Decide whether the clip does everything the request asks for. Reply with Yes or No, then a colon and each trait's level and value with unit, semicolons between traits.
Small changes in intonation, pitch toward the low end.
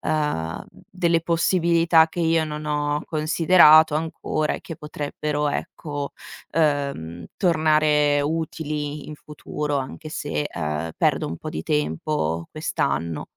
No: narrow, 1.9 semitones; medium, 150 Hz